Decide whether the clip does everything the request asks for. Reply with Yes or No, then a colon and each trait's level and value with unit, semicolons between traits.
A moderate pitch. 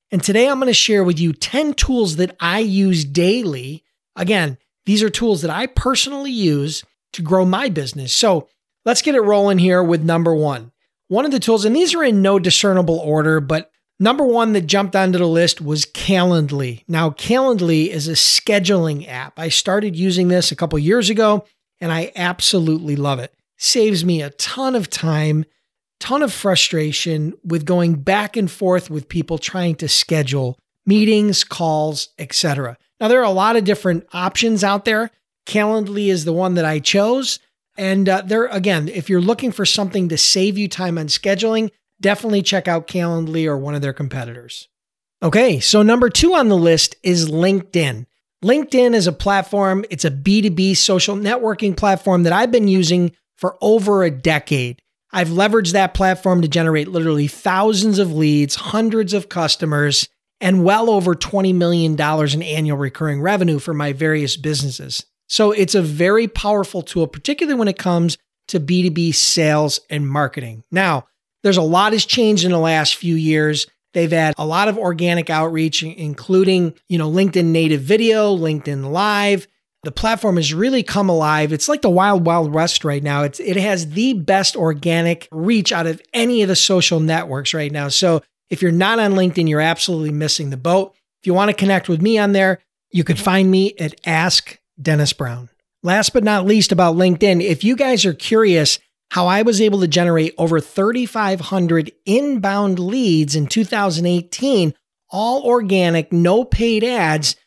Yes: medium, 180 Hz